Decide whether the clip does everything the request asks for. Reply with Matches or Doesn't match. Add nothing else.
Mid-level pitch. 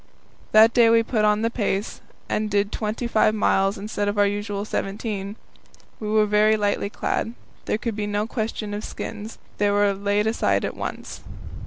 Doesn't match